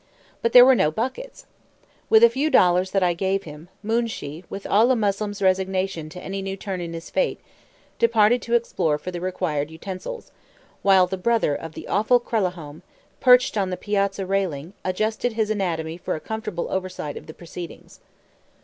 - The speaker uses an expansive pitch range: No, average, 4.0 semitones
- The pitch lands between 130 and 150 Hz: No, high, 195 Hz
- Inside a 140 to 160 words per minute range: No, average, 175 wpm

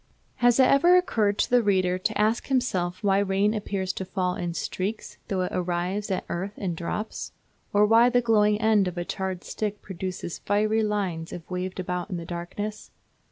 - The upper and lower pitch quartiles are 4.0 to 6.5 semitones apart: No, average, 2.9 semitones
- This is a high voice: Yes, high, 195 Hz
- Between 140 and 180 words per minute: No, average, 190 wpm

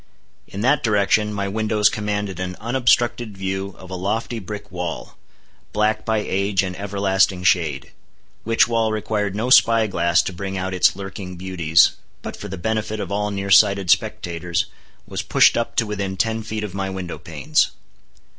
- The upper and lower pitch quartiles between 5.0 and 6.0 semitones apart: No, narrow, 2.5 semitones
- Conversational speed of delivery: Yes, average, 170 wpm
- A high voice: No, low, 100 Hz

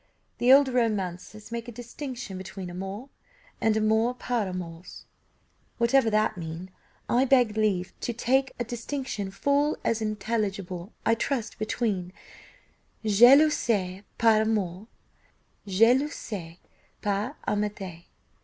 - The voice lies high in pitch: Yes, high, 215 Hz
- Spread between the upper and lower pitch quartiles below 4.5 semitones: Yes, average, 4.0 semitones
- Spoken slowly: Yes, slow, 115 wpm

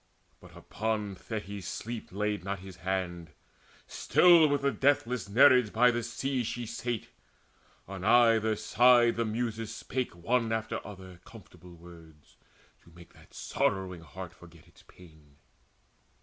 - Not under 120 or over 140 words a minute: Yes, slow, 135 wpm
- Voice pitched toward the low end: Yes, low, 105 Hz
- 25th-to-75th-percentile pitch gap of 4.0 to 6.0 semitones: Yes, average, 4.8 semitones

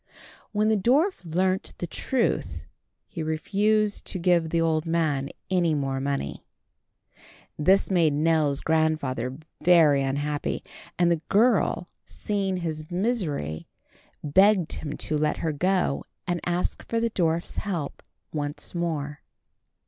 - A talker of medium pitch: Yes, medium, 165 Hz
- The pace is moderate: No, slow, 125 wpm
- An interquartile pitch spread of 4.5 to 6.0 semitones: No, average, 4.1 semitones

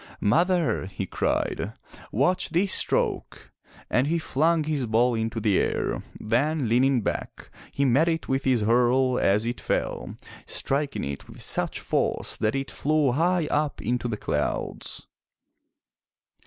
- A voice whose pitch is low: Yes, low, 130 Hz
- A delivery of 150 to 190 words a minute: No, average, 140 wpm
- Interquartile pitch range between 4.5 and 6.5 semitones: Yes, average, 5.1 semitones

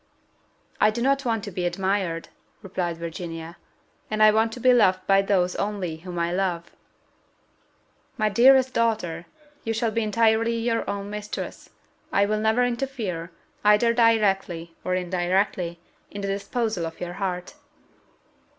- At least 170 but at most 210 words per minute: No, average, 145 wpm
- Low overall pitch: No, high, 200 Hz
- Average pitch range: Yes, average, 4.1 semitones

